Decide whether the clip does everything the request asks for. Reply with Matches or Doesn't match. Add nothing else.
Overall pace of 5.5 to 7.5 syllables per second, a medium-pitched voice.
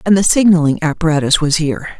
Matches